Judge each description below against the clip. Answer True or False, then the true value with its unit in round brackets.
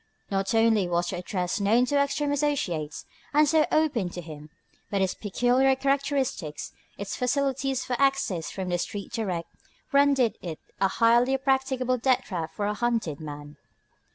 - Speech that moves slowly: False (155 wpm)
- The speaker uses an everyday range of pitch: False (6.9 semitones)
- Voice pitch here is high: True (230 Hz)